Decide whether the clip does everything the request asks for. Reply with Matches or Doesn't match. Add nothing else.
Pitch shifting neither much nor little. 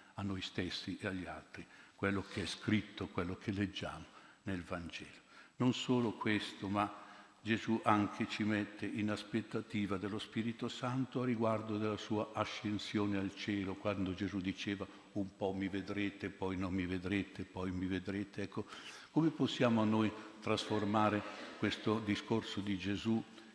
Doesn't match